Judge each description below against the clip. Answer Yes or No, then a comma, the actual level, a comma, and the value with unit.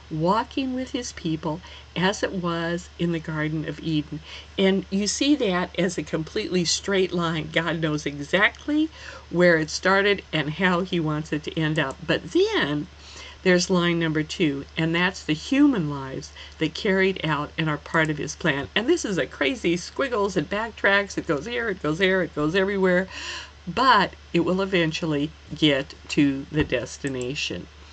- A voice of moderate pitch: Yes, medium, 170 Hz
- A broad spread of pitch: No, average, 3.8 semitones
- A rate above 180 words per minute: No, average, 170 wpm